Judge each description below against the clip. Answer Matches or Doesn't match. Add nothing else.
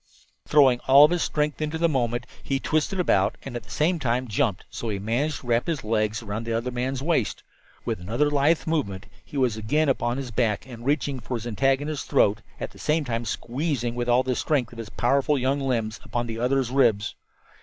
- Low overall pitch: Matches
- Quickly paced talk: Matches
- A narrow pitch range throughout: Doesn't match